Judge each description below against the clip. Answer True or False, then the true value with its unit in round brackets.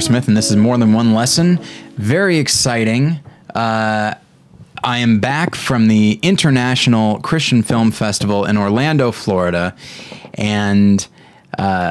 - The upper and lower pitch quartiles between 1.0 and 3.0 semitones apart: False (3.4 semitones)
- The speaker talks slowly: True (125 wpm)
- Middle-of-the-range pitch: False (115 Hz)